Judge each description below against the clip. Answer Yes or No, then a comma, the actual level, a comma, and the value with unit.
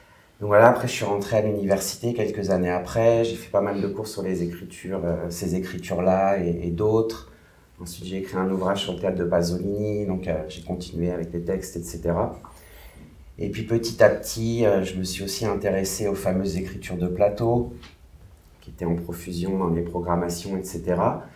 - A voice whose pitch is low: Yes, very low, 95 Hz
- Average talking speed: Yes, average, 190 wpm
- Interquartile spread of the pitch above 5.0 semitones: No, average, 2.8 semitones